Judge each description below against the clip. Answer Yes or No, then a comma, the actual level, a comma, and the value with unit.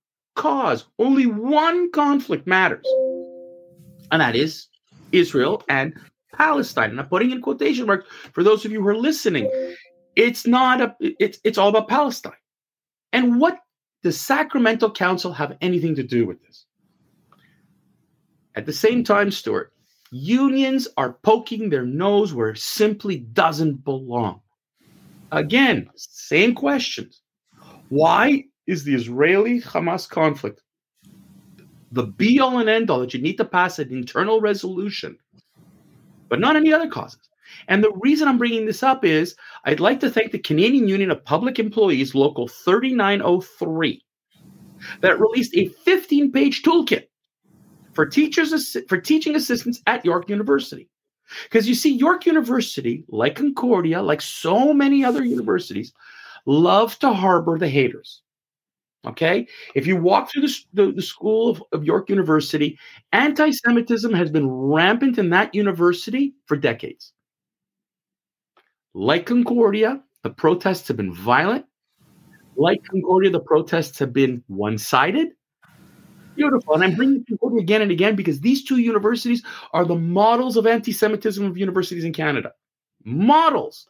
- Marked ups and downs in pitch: Yes, wide, 7.4 semitones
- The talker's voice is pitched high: Yes, high, 215 Hz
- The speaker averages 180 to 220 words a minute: No, average, 140 wpm